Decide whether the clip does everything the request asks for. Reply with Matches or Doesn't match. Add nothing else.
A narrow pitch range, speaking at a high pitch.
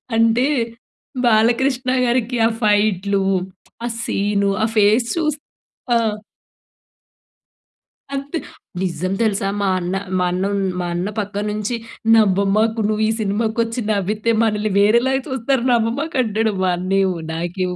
Doesn't match